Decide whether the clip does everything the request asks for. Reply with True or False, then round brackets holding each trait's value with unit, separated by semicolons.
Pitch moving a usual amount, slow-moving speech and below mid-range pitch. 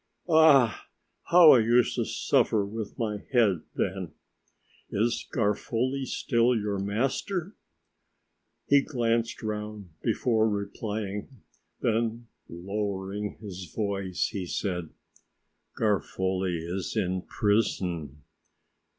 True (3.4 semitones; 95 wpm; 105 Hz)